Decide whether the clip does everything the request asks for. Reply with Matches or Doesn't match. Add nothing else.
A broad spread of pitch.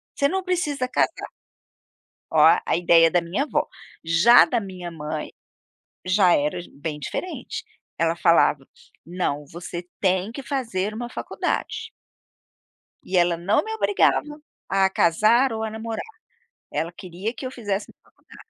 Matches